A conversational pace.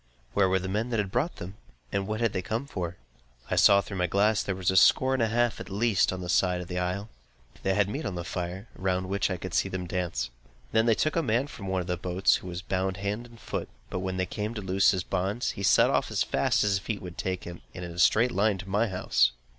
No: fast, 280 wpm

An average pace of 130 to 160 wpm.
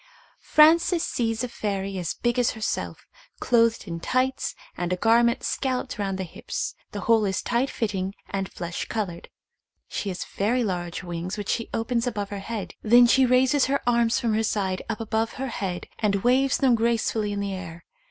No: average, 185 wpm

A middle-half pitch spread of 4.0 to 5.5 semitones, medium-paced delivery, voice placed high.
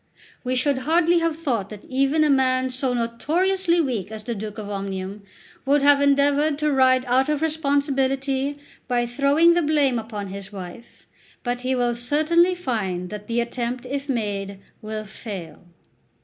Yes: average, 4.9 semitones; average, 165 wpm; very high, 255 Hz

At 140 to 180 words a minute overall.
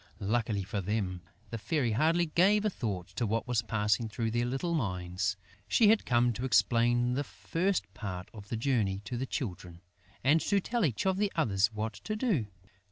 No: average, 190 wpm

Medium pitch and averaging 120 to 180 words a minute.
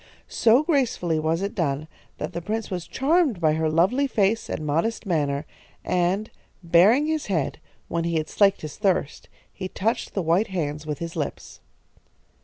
Yes: medium, 175 Hz; average, 170 wpm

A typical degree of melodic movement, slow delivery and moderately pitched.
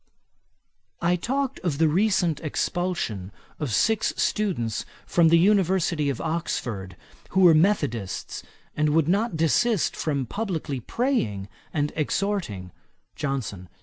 No: wide, 6.1 semitones; slow, 115 wpm; medium, 160 Hz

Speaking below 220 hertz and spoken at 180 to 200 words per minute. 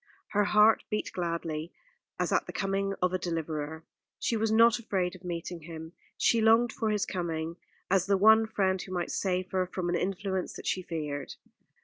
Yes: medium, 185 Hz; average, 190 wpm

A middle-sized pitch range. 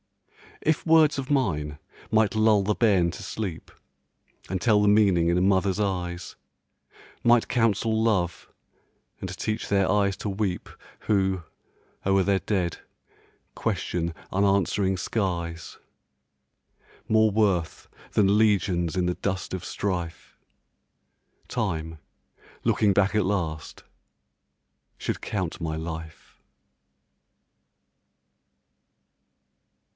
Yes: average, 3.4 semitones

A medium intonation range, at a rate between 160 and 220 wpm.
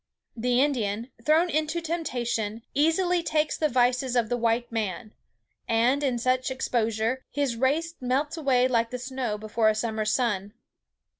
No: average, 4.0 semitones; average, 150 wpm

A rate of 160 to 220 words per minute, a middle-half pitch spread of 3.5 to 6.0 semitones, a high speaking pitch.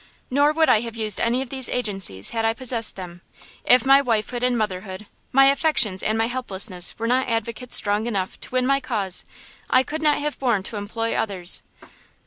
Yes: average, 195 wpm; average, 4.0 semitones; high, 230 Hz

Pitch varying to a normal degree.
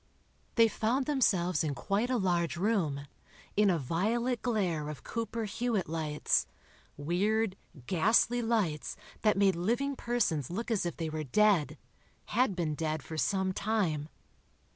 No: wide, 5.9 semitones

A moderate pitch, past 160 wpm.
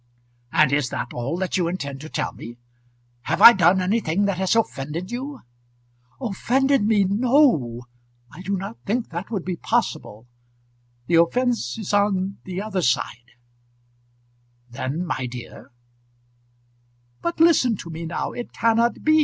No: medium, 180 Hz; average, 155 wpm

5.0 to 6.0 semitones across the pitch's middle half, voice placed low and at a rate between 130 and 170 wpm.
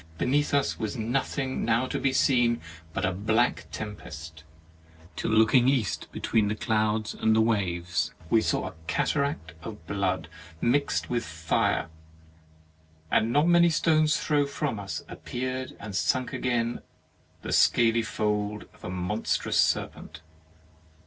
No: average, 4.2 semitones; low, 110 Hz; average, 140 wpm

